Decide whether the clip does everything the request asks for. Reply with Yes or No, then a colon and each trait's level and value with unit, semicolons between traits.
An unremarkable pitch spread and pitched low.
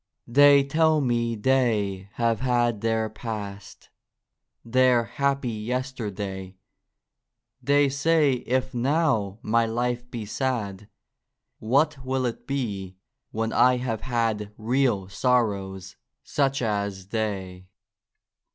Yes: average, 4.0 semitones; low, 115 Hz